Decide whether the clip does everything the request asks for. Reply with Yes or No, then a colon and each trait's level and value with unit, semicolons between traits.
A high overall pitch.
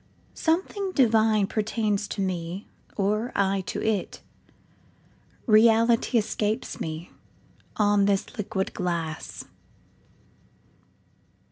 Yes: high, 210 Hz